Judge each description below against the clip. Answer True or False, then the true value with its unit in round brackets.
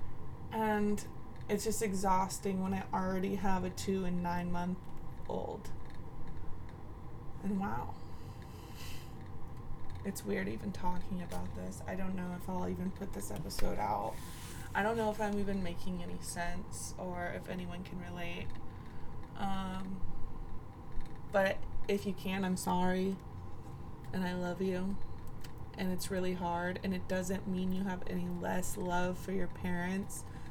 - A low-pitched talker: False (180 Hz)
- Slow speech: False (145 wpm)